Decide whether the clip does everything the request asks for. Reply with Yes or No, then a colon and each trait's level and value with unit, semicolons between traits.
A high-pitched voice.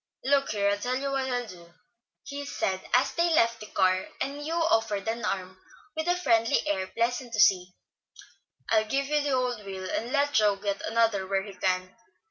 Yes: high, 225 Hz